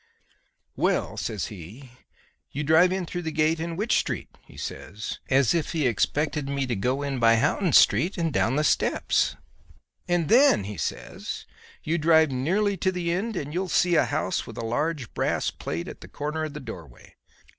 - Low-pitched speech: No, medium, 150 Hz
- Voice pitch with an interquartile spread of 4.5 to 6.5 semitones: Yes, average, 5.3 semitones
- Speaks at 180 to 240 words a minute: Yes, average, 190 wpm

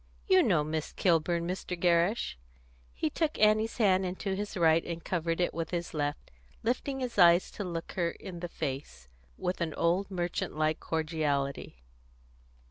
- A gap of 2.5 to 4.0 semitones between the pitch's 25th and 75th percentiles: Yes, average, 3.1 semitones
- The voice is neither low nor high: Yes, medium, 170 Hz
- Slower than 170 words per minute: Yes, average, 160 wpm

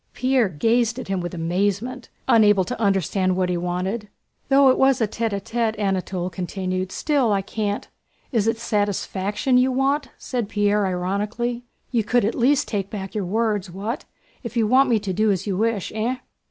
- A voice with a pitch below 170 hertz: No, high, 210 Hz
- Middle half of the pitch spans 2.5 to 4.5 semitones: Yes, average, 3.8 semitones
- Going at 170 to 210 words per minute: Yes, average, 180 wpm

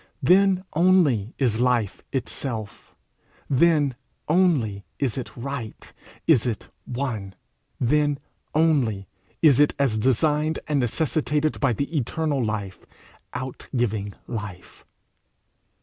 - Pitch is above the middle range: No, low, 130 Hz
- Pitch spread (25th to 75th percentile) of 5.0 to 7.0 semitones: Yes, average, 5.3 semitones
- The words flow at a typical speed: No, slow, 100 wpm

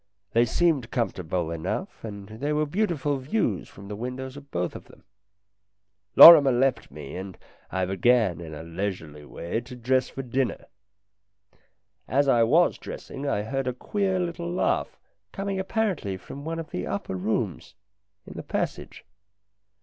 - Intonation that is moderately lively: No, wide, 7.2 semitones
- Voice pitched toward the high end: No, low, 125 Hz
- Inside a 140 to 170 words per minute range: Yes, average, 155 wpm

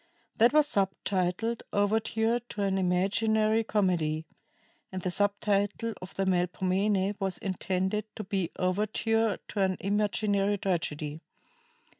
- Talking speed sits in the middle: No, slow, 120 wpm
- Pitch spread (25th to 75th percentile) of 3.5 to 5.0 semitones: No, narrow, 2.5 semitones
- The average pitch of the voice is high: Yes, high, 200 Hz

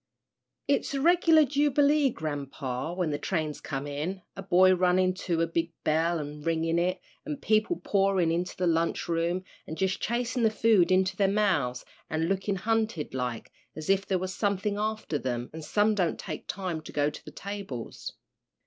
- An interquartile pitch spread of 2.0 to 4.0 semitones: No, average, 4.5 semitones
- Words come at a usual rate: Yes, average, 180 wpm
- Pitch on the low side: No, medium, 185 Hz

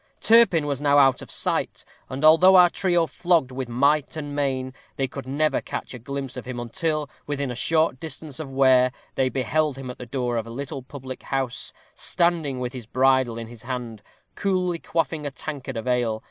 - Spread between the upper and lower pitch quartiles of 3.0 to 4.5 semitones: Yes, average, 3.5 semitones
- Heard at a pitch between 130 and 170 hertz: Yes, low, 135 Hz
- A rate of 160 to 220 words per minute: Yes, average, 200 wpm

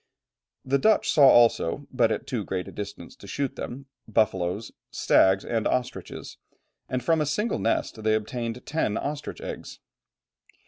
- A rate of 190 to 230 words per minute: No, average, 155 wpm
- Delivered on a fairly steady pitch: No, average, 4.3 semitones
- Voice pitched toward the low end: Yes, low, 120 Hz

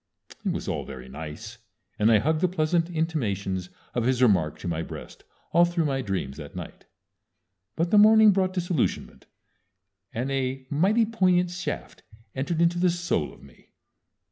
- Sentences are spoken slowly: No, average, 165 wpm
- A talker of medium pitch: Yes, medium, 150 Hz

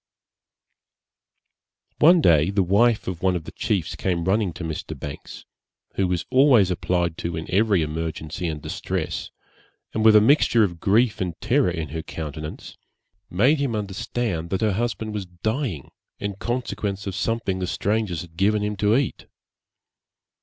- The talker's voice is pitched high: No, very low, 95 Hz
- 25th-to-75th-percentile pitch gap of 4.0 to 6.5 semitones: Yes, average, 4.5 semitones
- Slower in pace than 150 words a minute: No, average, 160 wpm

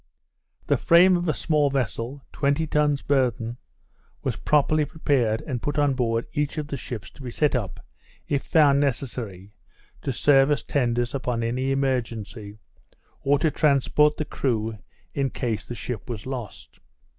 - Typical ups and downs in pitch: Yes, average, 3.8 semitones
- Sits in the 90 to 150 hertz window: Yes, low, 135 Hz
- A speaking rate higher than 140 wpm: Yes, average, 155 wpm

